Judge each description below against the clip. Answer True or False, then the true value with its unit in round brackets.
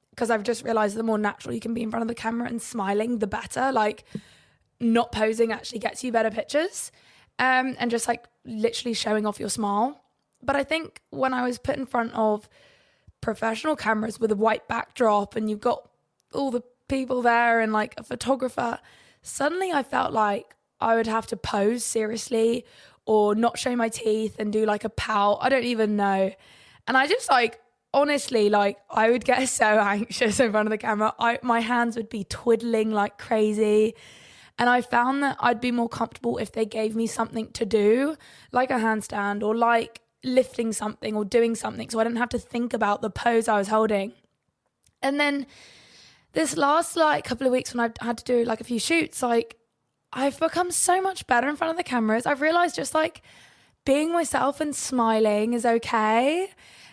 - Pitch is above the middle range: True (235 Hz)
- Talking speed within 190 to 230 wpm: True (195 wpm)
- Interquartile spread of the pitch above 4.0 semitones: False (2.7 semitones)